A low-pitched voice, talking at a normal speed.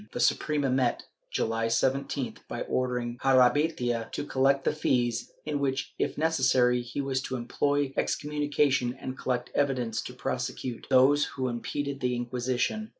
Yes: low, 130 Hz; average, 150 wpm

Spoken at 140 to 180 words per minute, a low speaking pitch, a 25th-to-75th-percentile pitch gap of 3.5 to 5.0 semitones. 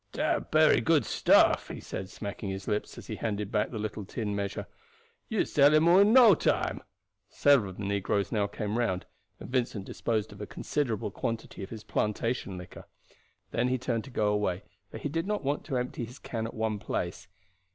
No: fast, 205 wpm; low, 110 Hz; average, 3.8 semitones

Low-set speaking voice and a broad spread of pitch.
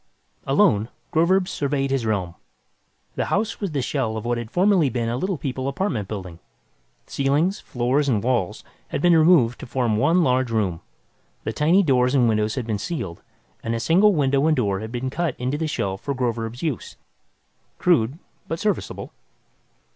Yes: low, 130 Hz; wide, 5.7 semitones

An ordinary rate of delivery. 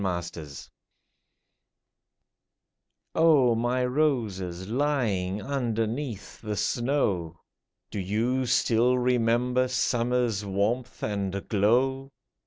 No: slow, 75 wpm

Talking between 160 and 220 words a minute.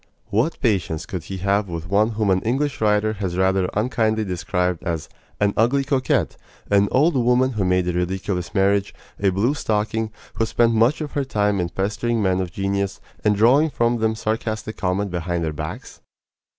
Yes: average, 180 wpm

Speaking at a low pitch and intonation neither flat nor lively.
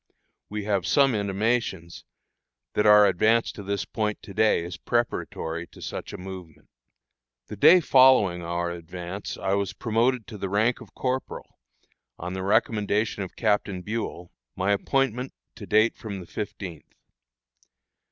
Yes: low, 100 Hz; average, 3.6 semitones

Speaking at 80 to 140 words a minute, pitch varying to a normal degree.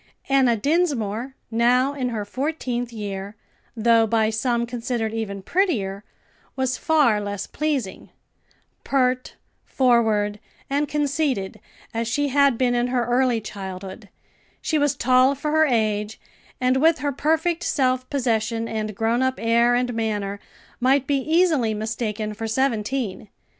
Yes: slow, 135 wpm; average, 3.9 semitones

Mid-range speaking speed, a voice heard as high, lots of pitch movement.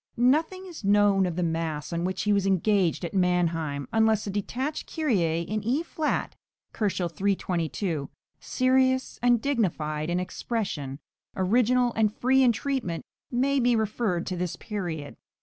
Yes: average, 150 wpm; high, 200 Hz; wide, 6.1 semitones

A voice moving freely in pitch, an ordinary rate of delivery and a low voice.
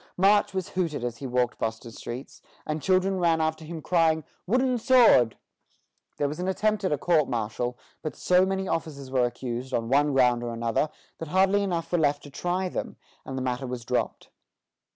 No: wide, 6.7 semitones; average, 195 wpm; medium, 155 Hz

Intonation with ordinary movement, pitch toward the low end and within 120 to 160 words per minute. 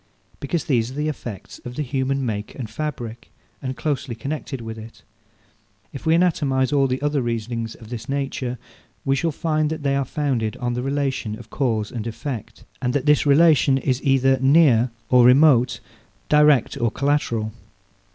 No: average, 3.4 semitones; low, 130 Hz; average, 170 wpm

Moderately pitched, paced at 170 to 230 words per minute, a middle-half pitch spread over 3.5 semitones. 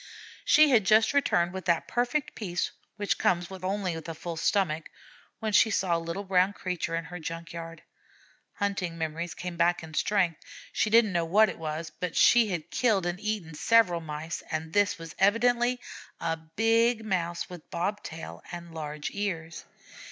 Yes: medium, 180 Hz; average, 175 wpm; average, 3.9 semitones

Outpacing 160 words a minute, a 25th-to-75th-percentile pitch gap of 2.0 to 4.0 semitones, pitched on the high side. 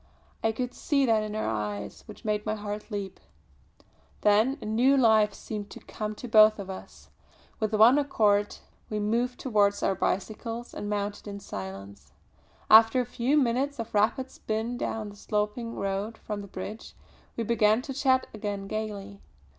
Yes: average, 170 wpm; narrow, 2.4 semitones; high, 215 Hz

